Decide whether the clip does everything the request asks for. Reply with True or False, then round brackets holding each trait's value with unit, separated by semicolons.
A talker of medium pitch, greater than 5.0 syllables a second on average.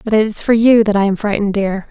False (210 Hz; 6.6 syllables/s)